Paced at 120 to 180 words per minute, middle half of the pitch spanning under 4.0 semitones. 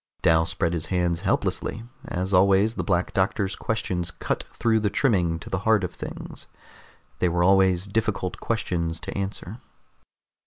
Yes: average, 155 wpm; average, 2.8 semitones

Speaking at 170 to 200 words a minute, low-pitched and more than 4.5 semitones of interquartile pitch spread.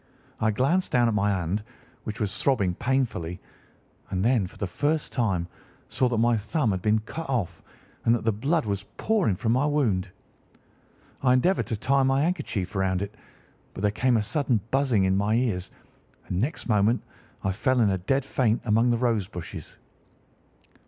Yes: average, 180 wpm; low, 115 Hz; average, 4.9 semitones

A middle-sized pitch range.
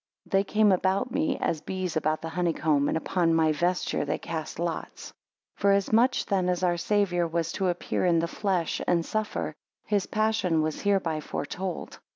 Yes: average, 3.4 semitones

